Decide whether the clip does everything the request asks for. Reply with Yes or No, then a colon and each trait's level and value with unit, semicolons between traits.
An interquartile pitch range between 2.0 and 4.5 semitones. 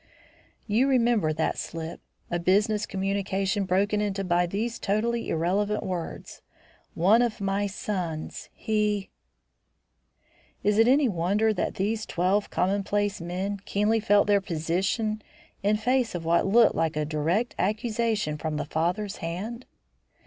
Yes: average, 3.4 semitones